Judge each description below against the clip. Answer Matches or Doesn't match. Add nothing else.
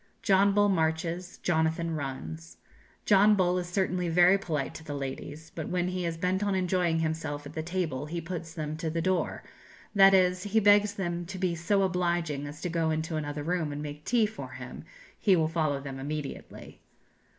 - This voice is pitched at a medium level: Matches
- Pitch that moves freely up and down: Doesn't match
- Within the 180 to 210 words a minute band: Matches